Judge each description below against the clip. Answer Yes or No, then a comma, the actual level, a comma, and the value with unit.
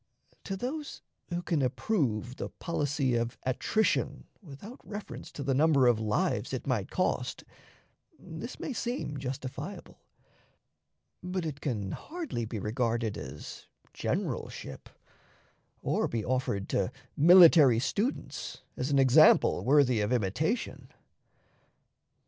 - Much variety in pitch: Yes, wide, 6.7 semitones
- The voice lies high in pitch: No, low, 135 Hz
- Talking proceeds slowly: Yes, slow, 115 wpm